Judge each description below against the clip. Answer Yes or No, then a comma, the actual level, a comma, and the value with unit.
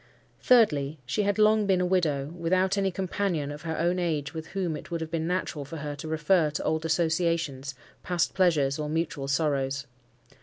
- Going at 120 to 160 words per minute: No, average, 190 wpm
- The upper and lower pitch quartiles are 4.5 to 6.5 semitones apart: No, average, 3.6 semitones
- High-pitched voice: No, medium, 160 Hz